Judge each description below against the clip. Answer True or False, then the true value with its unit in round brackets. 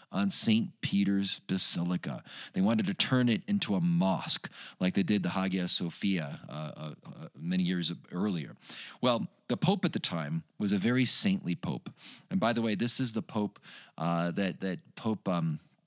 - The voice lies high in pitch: False (100 Hz)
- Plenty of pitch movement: True (8.4 semitones)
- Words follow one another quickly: False (180 wpm)